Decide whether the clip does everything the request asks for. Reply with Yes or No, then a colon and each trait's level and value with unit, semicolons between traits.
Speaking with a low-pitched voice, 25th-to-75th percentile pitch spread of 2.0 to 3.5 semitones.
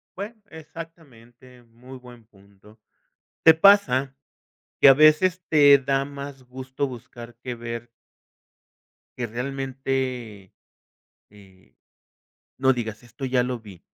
Yes: low, 130 Hz; average, 3.0 semitones